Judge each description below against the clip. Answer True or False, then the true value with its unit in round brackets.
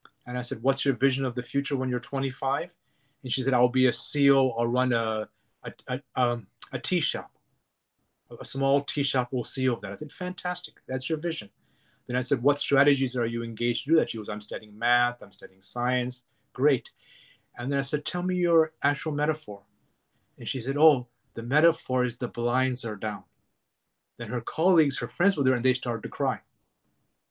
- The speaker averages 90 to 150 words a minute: False (205 wpm)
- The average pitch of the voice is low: True (130 Hz)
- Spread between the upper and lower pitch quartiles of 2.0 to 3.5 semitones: True (2.8 semitones)